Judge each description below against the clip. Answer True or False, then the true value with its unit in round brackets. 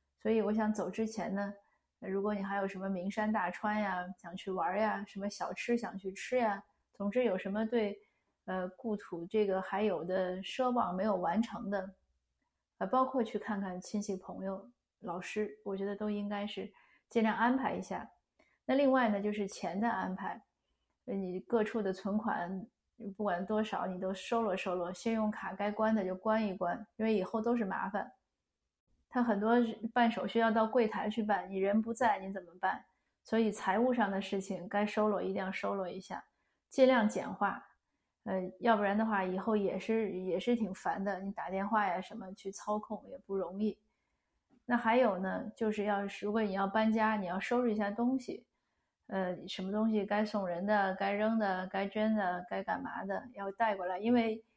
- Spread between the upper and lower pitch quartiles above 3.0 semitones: False (2.6 semitones)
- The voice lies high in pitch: True (205 Hz)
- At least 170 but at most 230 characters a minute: False (265 characters per minute)